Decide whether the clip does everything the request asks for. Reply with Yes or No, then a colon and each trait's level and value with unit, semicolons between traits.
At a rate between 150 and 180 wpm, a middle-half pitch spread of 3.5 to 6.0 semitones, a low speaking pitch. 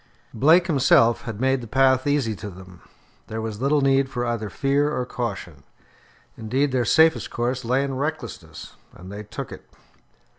Yes: average, 170 wpm; average, 4.0 semitones; low, 125 Hz